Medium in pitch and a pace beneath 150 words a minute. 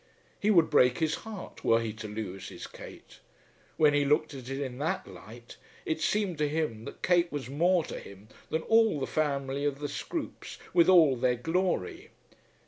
No: medium, 145 Hz; average, 190 wpm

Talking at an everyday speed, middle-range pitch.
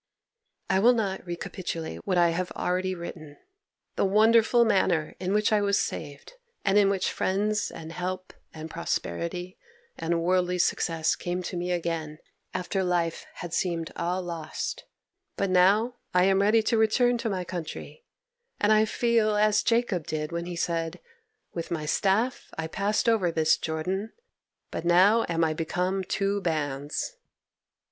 Yes: average, 155 wpm; medium, 180 Hz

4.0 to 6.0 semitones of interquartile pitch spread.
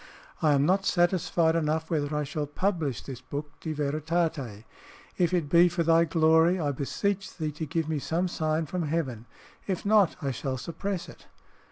No: average, 3.0 semitones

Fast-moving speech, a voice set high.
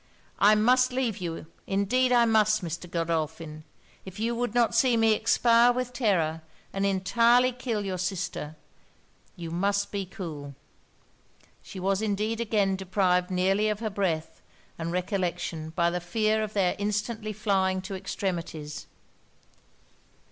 No: average, 140 wpm; high, 195 Hz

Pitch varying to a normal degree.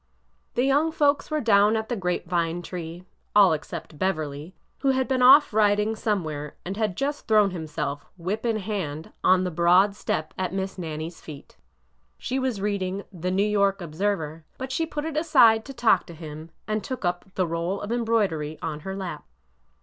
Yes: average, 5.0 semitones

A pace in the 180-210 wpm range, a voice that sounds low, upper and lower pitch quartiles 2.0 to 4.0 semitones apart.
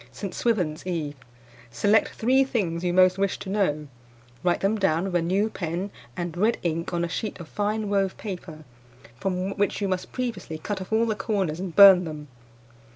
No: average, 190 wpm; medium, 185 Hz; average, 3.3 semitones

